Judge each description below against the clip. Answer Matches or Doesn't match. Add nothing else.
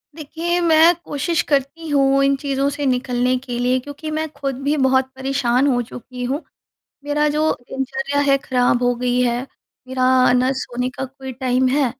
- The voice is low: Doesn't match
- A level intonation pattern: Matches